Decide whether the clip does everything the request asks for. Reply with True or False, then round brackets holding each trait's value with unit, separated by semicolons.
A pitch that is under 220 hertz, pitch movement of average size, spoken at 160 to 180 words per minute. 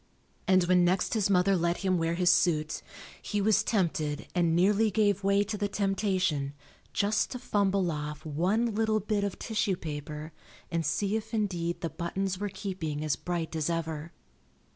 True (185 Hz; 3.6 semitones; 170 wpm)